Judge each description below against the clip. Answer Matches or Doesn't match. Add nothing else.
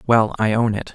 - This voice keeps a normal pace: Doesn't match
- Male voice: Matches